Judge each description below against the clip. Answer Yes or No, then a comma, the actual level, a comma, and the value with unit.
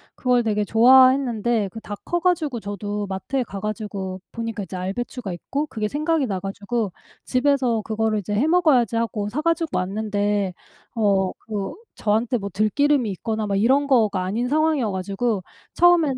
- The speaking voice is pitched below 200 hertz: No, high, 225 Hz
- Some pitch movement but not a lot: Yes, average, 4.5 semitones